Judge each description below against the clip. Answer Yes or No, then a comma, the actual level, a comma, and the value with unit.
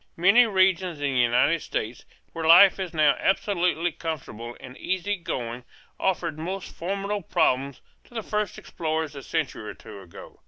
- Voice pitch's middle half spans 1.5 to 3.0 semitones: No, wide, 5.6 semitones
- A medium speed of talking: Yes, average, 155 wpm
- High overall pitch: No, medium, 165 Hz